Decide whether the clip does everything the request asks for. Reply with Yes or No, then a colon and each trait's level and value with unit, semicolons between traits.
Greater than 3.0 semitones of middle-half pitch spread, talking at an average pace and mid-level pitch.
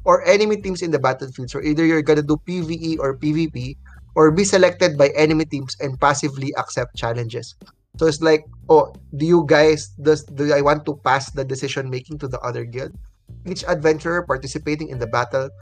Yes: average, 3.5 semitones; average, 190 wpm; medium, 145 Hz